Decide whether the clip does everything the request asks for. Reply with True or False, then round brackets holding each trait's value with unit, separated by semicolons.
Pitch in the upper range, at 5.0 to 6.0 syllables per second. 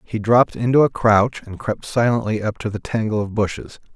False (110 Hz; 5.4 syllables/s)